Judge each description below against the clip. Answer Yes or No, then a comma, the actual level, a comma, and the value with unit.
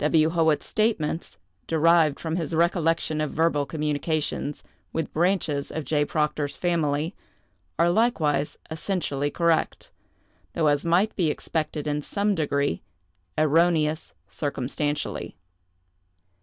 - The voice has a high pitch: No, medium, 155 Hz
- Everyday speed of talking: No, slow, 110 wpm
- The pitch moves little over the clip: Yes, narrow, 2.3 semitones